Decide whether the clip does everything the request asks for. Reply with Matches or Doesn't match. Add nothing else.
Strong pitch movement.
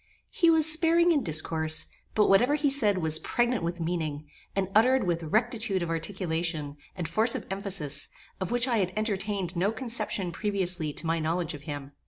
Matches